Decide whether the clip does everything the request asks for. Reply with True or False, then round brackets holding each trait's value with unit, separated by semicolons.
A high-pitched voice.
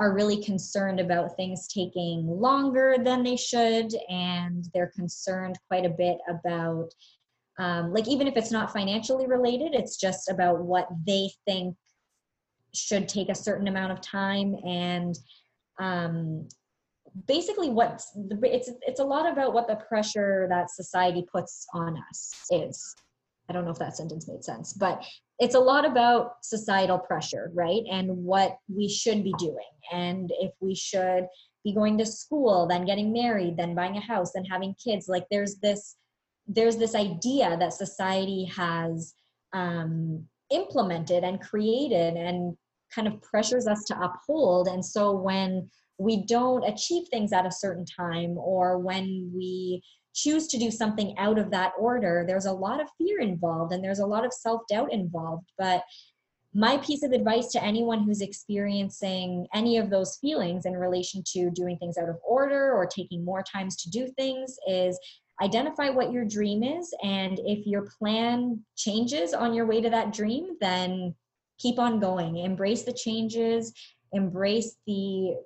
True (195 Hz)